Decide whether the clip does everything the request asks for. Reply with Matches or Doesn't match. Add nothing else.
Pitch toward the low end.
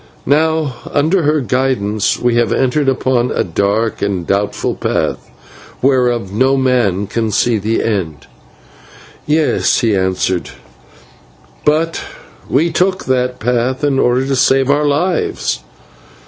Matches